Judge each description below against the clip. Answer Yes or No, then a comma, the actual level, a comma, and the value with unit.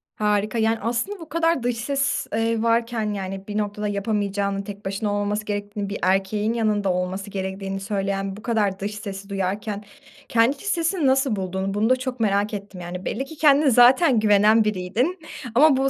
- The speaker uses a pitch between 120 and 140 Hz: No, high, 210 Hz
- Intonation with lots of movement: No, average, 3.2 semitones